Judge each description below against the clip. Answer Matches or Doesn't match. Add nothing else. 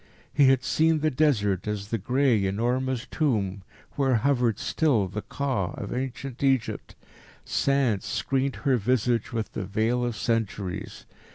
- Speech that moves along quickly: Doesn't match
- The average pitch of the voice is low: Matches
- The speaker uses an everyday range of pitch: Matches